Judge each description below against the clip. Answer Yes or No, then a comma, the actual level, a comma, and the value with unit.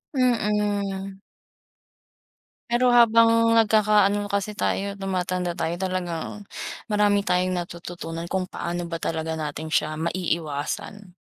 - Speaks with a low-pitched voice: No, high, 190 Hz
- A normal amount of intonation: Yes, average, 3.4 semitones